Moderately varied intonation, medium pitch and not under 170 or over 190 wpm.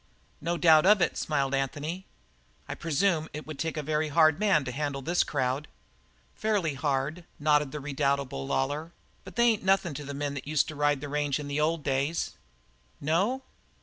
Yes: average, 3.0 semitones; medium, 150 Hz; average, 185 wpm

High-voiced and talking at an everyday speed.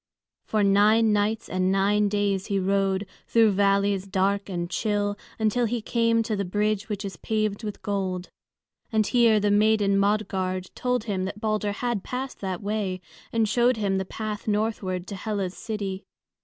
Yes: high, 205 Hz; average, 170 wpm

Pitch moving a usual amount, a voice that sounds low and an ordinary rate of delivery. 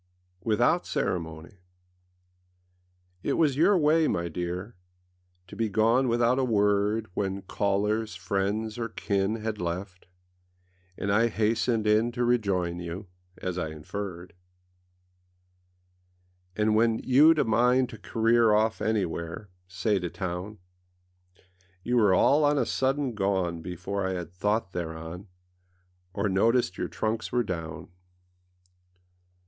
No: average, 4.1 semitones; low, 105 Hz; slow, 120 wpm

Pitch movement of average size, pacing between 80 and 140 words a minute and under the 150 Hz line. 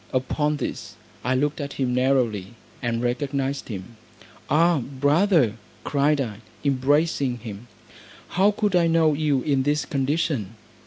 Yes: average, 3.5 semitones; slow, 135 wpm; medium, 140 Hz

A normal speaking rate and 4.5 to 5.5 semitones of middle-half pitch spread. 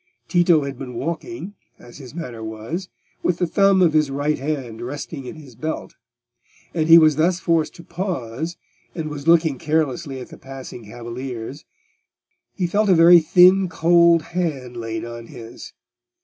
Yes: average, 165 wpm; average, 5.1 semitones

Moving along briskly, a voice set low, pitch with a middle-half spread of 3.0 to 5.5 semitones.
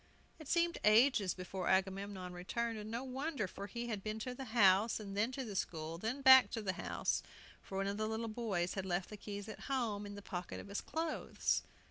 No: fast, 215 wpm; high, 210 Hz; average, 3.7 semitones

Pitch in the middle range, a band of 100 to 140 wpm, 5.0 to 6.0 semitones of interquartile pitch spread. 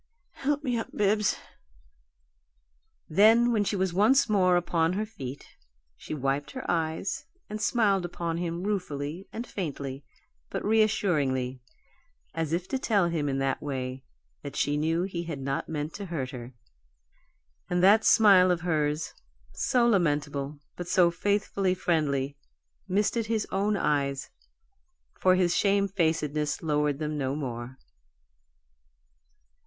Yes: medium, 170 Hz; slow, 135 wpm; wide, 5.6 semitones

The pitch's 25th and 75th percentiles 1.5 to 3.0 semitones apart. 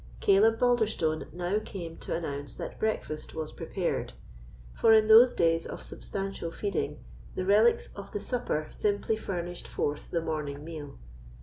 No: average, 5.1 semitones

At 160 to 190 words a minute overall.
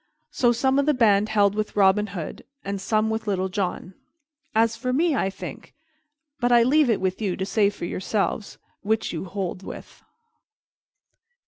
Yes: average, 175 wpm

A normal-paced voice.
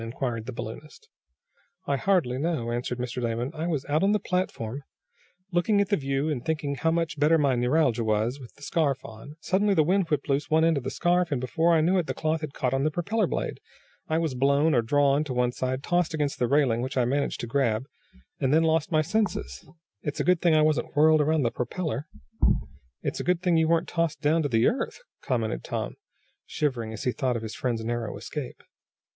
No: fast, 225 wpm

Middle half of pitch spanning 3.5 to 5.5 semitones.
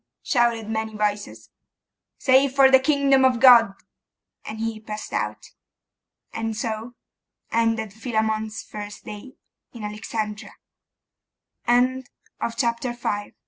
No: narrow, 2.6 semitones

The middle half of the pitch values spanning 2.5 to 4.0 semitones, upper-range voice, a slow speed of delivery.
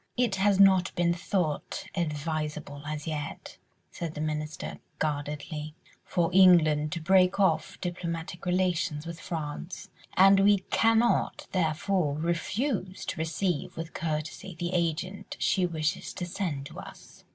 No: average, 3.4 semitones; medium, 170 Hz; slow, 130 wpm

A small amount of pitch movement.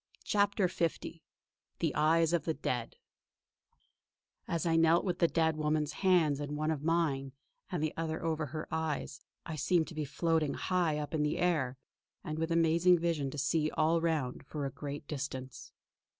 Yes: narrow, 2.1 semitones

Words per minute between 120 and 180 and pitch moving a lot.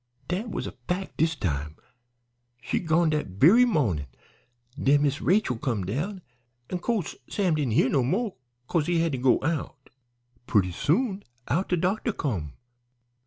Yes: average, 160 wpm; wide, 6.7 semitones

